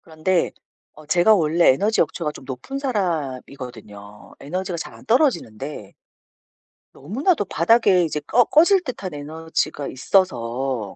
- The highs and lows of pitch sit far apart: Yes, wide, 6.9 semitones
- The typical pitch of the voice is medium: Yes, medium, 160 Hz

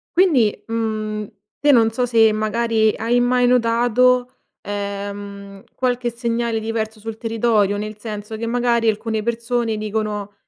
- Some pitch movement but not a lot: No, narrow, 2.0 semitones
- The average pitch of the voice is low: No, high, 225 Hz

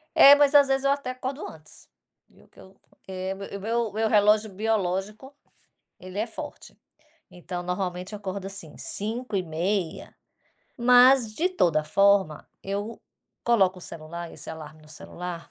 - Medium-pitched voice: No, high, 200 Hz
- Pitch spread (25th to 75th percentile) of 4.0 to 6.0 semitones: Yes, average, 4.6 semitones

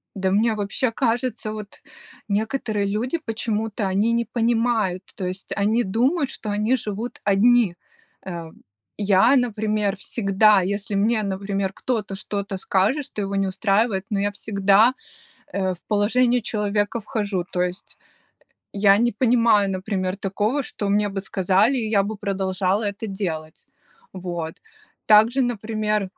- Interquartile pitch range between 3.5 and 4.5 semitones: No, narrow, 2.5 semitones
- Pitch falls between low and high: No, high, 205 Hz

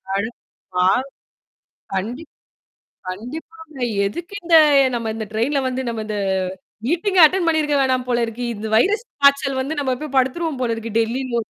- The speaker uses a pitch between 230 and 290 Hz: Yes, very high, 260 Hz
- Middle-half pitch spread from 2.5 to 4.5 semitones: No, wide, 5.6 semitones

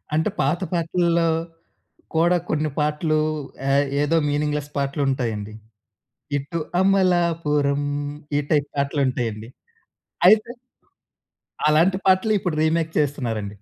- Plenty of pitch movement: No, average, 3.3 semitones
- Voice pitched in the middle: Yes, medium, 150 Hz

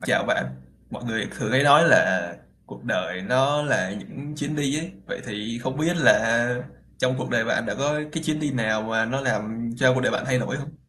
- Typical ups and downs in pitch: Yes, average, 4.4 semitones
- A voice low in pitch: Yes, low, 130 Hz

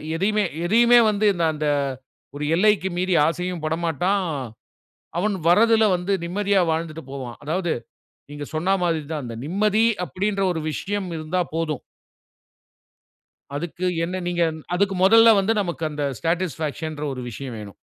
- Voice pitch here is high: No, medium, 175 Hz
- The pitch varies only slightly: No, average, 4.2 semitones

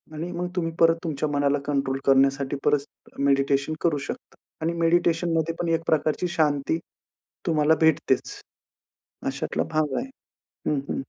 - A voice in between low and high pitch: Yes, medium, 155 Hz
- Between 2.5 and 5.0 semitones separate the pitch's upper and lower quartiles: Yes, average, 2.8 semitones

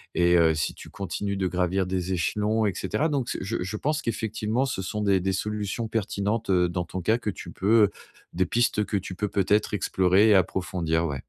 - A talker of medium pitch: No, low, 100 Hz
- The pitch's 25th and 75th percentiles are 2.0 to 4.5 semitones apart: Yes, average, 3.0 semitones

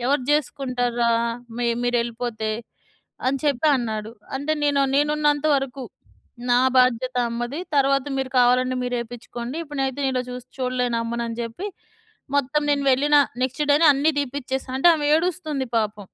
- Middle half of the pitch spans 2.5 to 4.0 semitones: Yes, average, 2.9 semitones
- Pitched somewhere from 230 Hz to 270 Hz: Yes, very high, 255 Hz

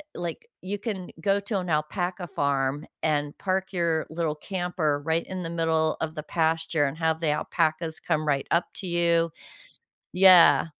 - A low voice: No, medium, 165 Hz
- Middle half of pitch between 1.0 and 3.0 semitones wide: Yes, narrow, 2.4 semitones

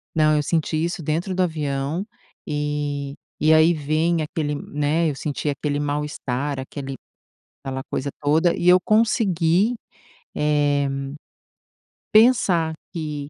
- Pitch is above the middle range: No, medium, 150 Hz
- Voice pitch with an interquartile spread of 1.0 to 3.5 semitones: Yes, average, 2.7 semitones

